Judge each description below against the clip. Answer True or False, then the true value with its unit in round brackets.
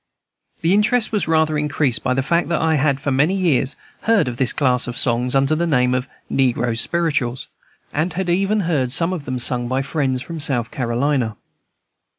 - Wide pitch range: False (4.8 semitones)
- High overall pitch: False (140 Hz)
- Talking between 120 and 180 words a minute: False (190 wpm)